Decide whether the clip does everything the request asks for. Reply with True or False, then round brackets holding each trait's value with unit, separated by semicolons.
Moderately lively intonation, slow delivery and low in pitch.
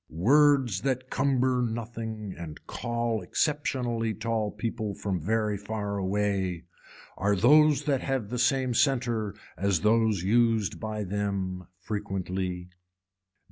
True (3.5 semitones; 115 wpm; 110 Hz)